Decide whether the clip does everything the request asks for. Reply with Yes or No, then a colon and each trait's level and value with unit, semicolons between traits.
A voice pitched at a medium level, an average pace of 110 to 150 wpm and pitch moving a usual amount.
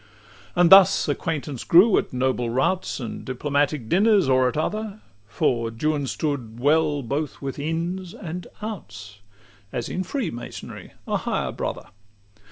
No: medium, 145 Hz; average, 140 wpm; wide, 5.9 semitones